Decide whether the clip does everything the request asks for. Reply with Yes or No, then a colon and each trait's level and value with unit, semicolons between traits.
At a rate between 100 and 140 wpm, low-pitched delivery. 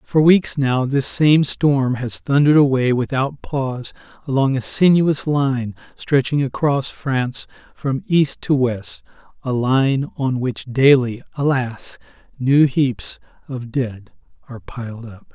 Yes: slow, 135 wpm; low, 130 Hz